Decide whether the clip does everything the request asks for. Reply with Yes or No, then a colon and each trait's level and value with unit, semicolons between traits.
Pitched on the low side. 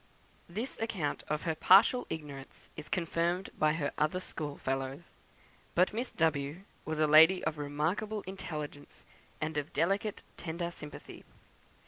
No: medium, 160 Hz